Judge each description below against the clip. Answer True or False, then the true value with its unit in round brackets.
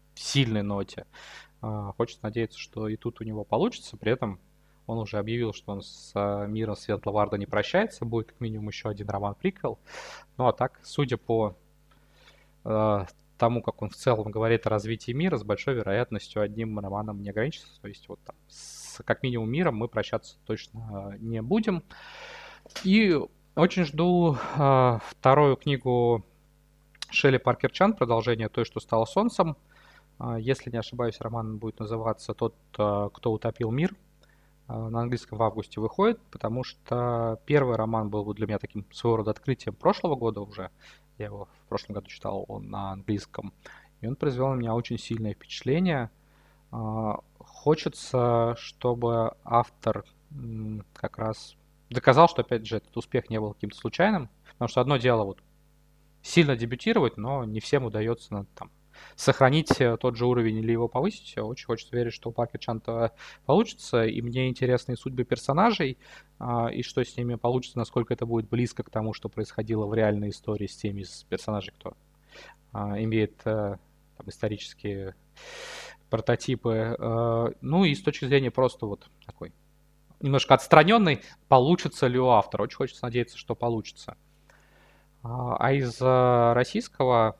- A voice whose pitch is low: True (120 Hz)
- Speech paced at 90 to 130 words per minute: False (150 wpm)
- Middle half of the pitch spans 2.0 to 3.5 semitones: False (4.0 semitones)